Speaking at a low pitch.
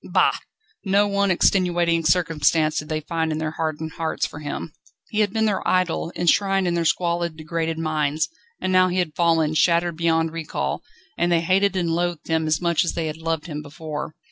No: medium, 165 Hz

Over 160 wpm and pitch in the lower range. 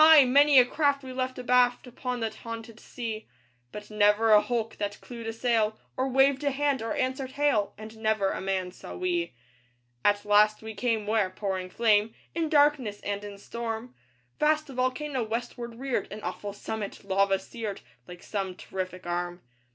No: average, 175 wpm; high, 225 Hz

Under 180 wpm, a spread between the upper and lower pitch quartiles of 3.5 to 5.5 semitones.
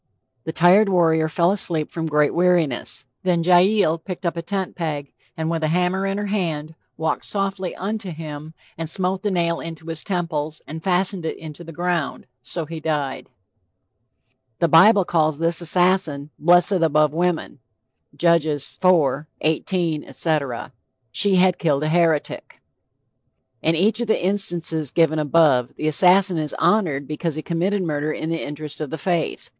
No: average, 160 wpm; average, 2.8 semitones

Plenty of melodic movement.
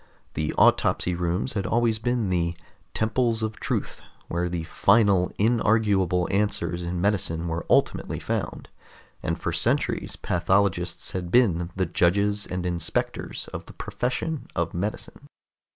No: average, 3.9 semitones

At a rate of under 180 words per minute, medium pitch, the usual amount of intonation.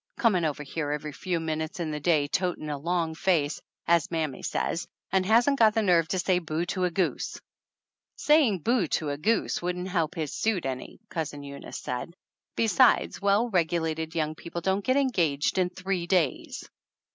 No: average, 185 wpm; medium, 170 Hz; average, 3.5 semitones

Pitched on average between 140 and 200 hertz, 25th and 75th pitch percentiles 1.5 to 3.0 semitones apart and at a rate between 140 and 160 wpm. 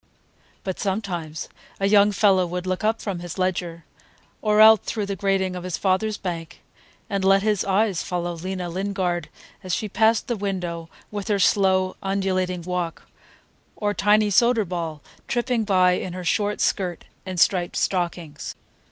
Yes: high, 190 Hz; narrow, 2.5 semitones; average, 155 wpm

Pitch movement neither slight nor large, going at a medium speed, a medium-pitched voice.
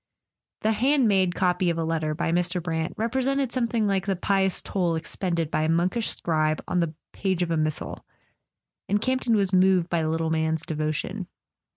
Yes: average, 3.8 semitones; average, 190 wpm; medium, 180 Hz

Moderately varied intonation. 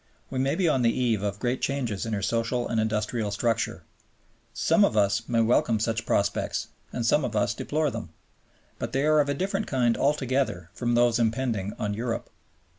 Yes: average, 3.3 semitones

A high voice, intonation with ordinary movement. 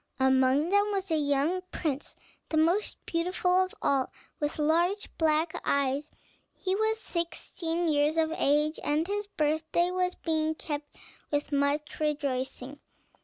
Yes: very high, 315 Hz; average, 3.4 semitones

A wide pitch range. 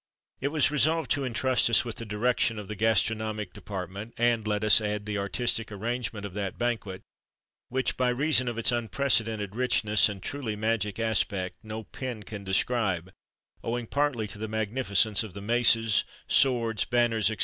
No: average, 2.7 semitones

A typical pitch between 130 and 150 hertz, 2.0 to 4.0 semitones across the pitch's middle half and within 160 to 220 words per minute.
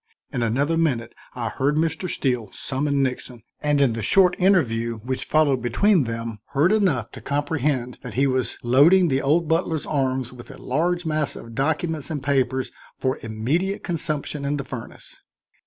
No: medium, 140 Hz; average, 4.4 semitones; average, 170 wpm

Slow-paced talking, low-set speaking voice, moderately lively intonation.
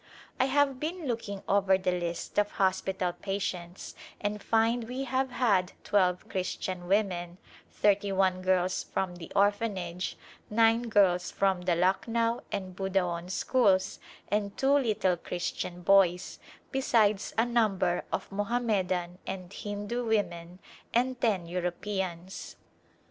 No: slow, 130 wpm; high, 195 Hz; average, 3.7 semitones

